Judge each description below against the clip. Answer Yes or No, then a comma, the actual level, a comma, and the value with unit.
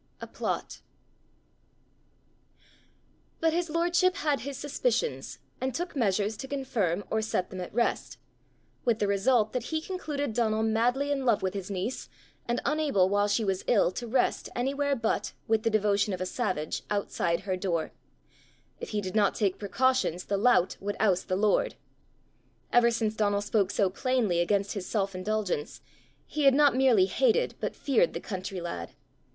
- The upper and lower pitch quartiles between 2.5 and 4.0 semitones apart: No, average, 5.2 semitones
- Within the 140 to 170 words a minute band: Yes, average, 165 wpm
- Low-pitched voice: No, high, 220 Hz